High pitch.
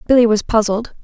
Yes: high, 225 Hz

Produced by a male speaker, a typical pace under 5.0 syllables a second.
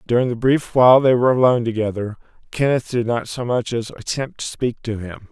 No: male; 5.8 syllables/s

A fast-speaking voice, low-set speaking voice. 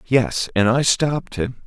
No: average, 180 wpm; low, 120 Hz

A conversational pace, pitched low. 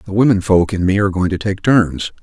No: fast, 270 wpm; very low, 95 Hz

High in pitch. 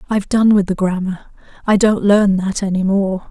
Yes: high, 195 Hz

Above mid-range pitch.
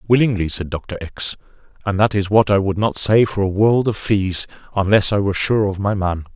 No: low, 100 Hz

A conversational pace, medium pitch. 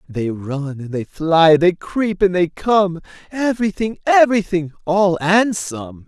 Yes: average, 150 wpm; medium, 180 Hz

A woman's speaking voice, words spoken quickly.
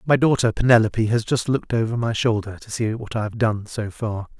No: male; fast, 230 wpm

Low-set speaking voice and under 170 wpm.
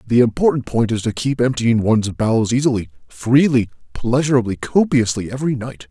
Yes: low, 120 Hz; average, 150 wpm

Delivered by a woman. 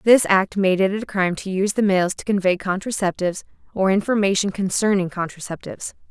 Yes: female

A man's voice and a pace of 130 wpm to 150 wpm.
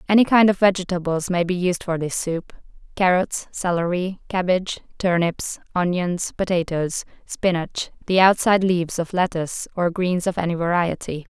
No: female; average, 145 wpm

